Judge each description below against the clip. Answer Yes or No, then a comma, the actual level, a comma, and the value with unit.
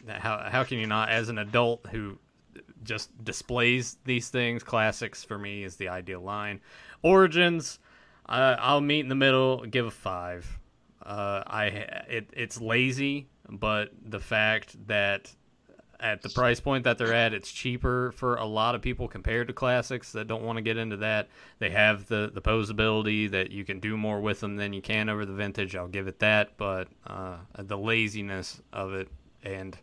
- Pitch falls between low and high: No, low, 110 Hz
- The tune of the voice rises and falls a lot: No, average, 3.2 semitones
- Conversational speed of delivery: Yes, average, 185 wpm